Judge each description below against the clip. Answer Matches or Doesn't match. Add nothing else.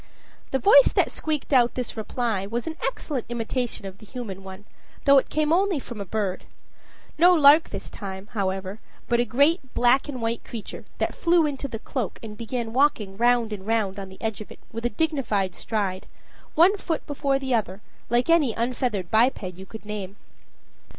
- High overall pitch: Matches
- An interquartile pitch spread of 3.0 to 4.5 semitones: Doesn't match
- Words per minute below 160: Doesn't match